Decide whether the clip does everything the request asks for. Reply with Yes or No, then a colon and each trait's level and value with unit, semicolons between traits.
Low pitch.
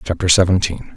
Yes: very low, 85 Hz